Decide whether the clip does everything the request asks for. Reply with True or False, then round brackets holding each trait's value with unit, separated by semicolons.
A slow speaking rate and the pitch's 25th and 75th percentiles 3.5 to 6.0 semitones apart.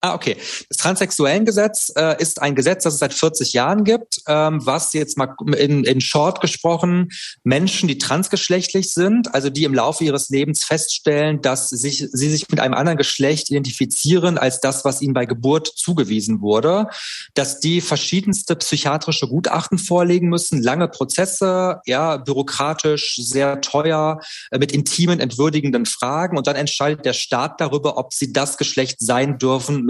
False (155 wpm; 3.8 semitones)